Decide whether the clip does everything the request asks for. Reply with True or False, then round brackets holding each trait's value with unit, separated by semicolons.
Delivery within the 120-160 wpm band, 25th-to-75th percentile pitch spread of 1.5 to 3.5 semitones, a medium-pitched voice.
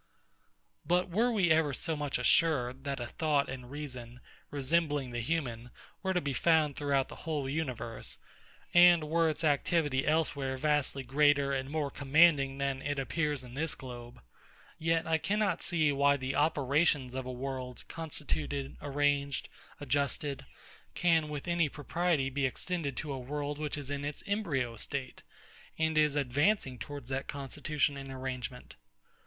True (155 wpm; 3.0 semitones; 145 Hz)